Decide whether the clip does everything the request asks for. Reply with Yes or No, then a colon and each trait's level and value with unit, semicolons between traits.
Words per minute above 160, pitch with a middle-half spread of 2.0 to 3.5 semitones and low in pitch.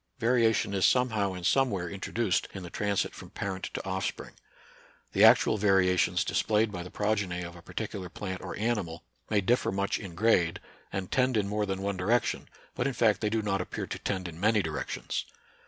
Yes: average, 195 wpm; average, 3.1 semitones; low, 100 Hz